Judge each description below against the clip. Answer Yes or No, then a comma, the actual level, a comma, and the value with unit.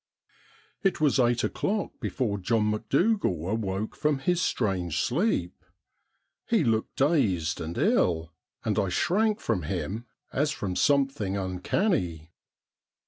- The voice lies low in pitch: Yes, low, 110 Hz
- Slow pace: Yes, slow, 120 wpm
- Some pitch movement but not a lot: No, wide, 8.6 semitones